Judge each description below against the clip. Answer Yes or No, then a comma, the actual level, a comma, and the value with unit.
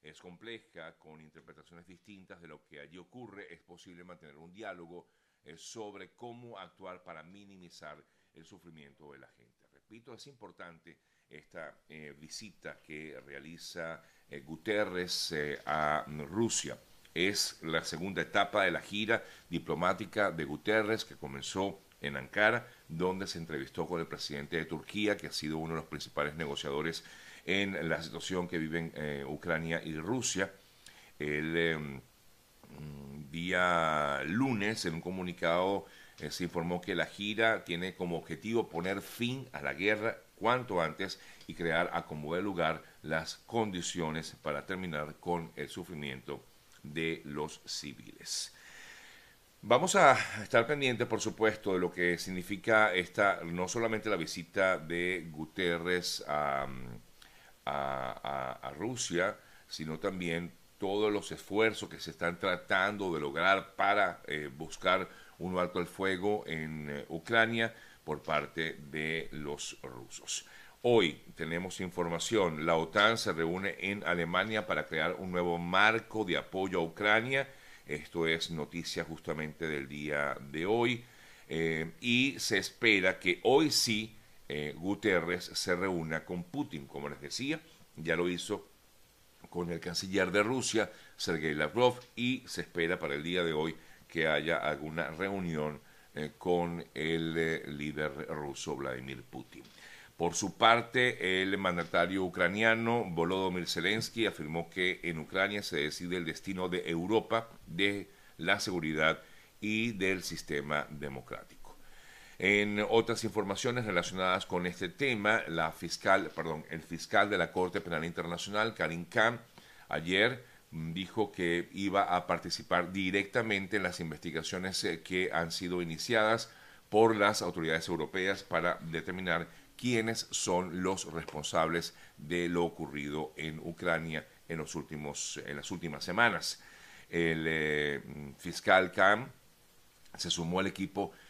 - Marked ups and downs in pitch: No, average, 3.9 semitones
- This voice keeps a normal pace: Yes, average, 140 wpm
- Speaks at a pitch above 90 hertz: No, very low, 85 Hz